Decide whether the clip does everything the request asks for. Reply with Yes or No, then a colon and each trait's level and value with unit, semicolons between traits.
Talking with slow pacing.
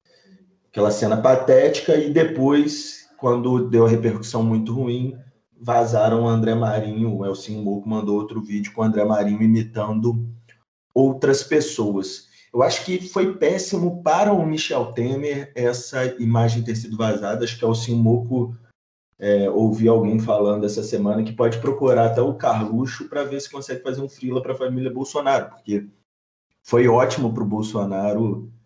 No: average, 155 wpm